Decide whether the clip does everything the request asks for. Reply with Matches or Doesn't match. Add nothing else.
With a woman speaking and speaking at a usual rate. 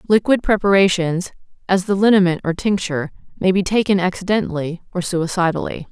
Doesn't match